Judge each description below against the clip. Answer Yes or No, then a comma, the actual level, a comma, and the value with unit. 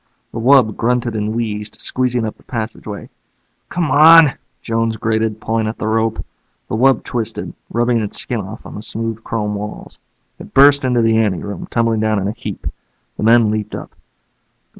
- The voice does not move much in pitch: Yes, narrow, 1.9 semitones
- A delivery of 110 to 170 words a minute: No, average, 180 wpm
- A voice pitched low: Yes, low, 115 Hz